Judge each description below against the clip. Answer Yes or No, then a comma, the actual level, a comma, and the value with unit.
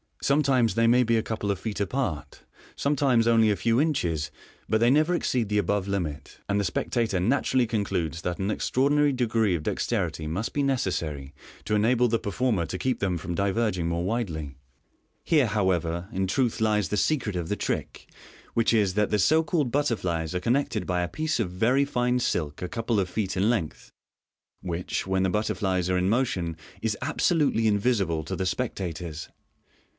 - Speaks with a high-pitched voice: No, low, 105 Hz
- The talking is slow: No, average, 190 wpm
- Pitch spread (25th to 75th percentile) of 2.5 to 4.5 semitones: No, average, 5.2 semitones